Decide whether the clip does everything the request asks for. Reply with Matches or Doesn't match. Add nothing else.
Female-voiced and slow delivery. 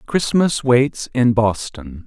Doesn't match